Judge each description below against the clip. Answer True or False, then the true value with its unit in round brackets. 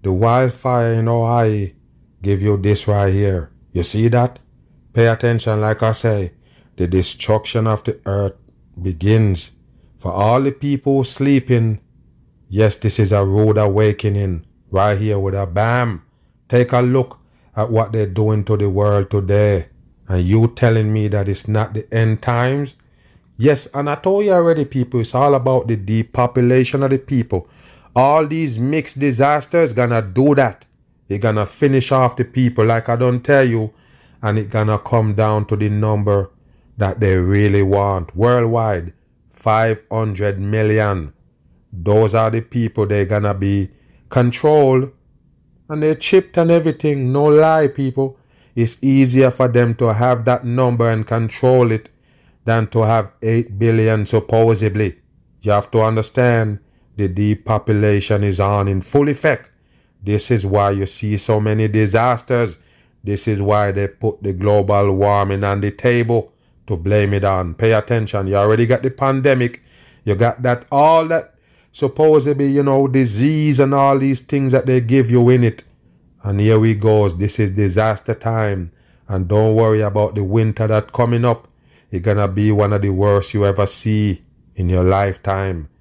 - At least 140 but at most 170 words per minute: True (160 wpm)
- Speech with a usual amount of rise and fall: True (3.6 semitones)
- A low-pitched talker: True (110 Hz)